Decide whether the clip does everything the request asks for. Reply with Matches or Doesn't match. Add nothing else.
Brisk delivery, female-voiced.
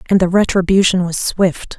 Doesn't match